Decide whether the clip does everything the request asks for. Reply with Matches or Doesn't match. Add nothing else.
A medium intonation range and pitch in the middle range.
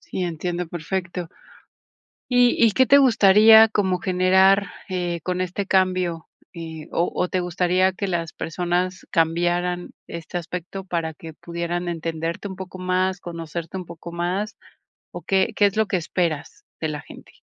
Doesn't match